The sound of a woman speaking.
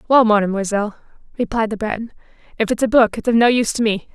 Yes: female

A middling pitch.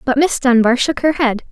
No: very high, 260 Hz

